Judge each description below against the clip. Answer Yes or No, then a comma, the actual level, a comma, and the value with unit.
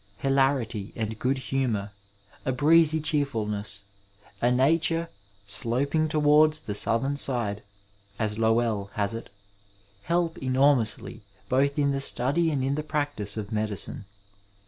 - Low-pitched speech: Yes, low, 130 Hz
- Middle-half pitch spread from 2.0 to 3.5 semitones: No, average, 5.1 semitones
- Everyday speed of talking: No, slow, 125 wpm